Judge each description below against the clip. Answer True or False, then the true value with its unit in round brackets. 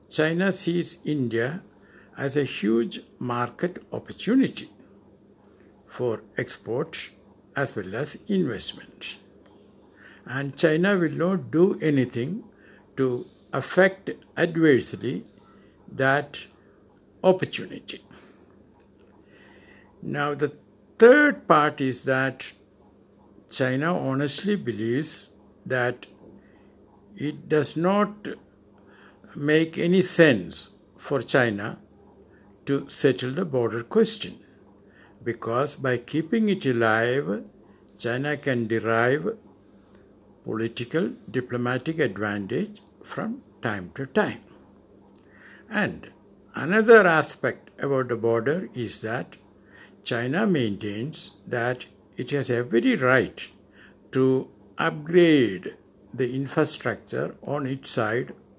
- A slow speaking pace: True (85 wpm)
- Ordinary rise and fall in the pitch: False (5.9 semitones)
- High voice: False (135 Hz)